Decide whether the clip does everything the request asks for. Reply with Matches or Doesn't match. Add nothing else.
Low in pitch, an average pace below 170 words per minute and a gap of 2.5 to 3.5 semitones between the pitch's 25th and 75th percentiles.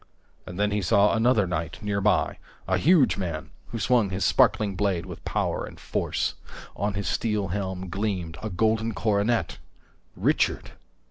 Matches